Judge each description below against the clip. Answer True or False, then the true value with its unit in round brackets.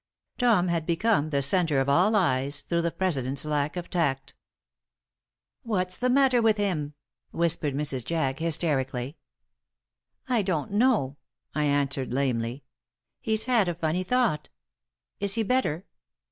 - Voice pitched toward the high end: False (165 Hz)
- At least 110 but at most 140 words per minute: True (135 wpm)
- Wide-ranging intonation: True (6.2 semitones)